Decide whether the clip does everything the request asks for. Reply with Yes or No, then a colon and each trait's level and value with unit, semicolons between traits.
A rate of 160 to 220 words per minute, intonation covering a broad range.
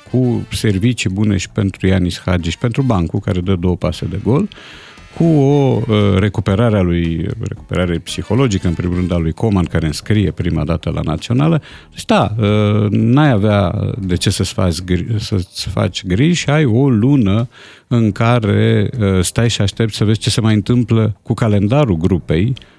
No: fast, 170 wpm; average, 4.1 semitones